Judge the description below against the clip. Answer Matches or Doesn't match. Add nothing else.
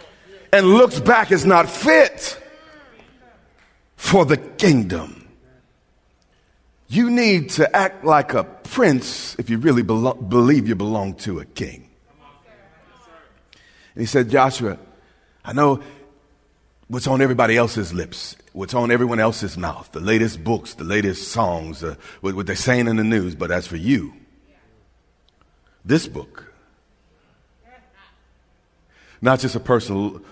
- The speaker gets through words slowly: Matches